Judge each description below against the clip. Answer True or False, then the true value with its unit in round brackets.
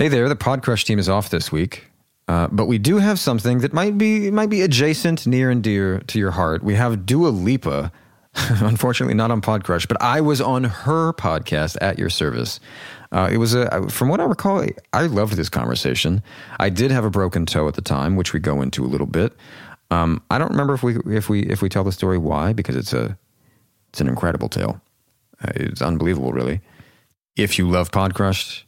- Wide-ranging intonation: True (6.1 semitones)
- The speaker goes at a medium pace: False (210 wpm)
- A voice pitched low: True (105 Hz)